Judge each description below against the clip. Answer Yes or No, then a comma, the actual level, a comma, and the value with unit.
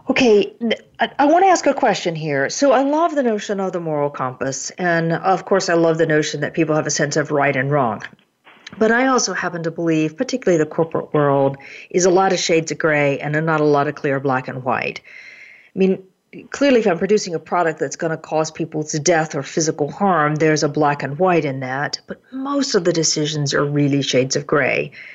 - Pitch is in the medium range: Yes, medium, 165 Hz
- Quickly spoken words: Yes, fast, 225 wpm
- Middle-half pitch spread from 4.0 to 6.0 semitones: Yes, average, 4.7 semitones